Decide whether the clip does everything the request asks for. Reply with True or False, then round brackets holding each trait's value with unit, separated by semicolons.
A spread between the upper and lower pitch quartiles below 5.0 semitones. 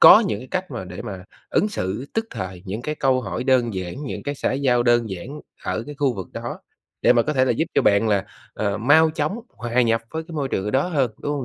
False (5.5 semitones)